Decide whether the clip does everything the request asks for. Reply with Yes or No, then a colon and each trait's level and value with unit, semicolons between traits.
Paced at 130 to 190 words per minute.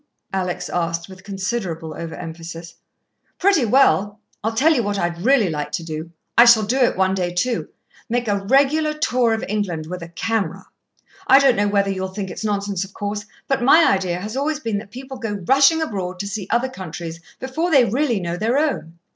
No: average, 200 wpm